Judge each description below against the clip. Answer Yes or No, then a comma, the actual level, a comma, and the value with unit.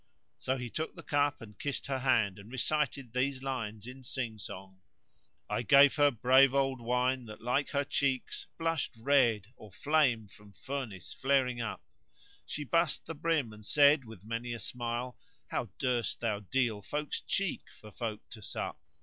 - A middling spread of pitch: Yes, average, 3.8 semitones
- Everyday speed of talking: Yes, average, 175 wpm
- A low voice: Yes, low, 125 Hz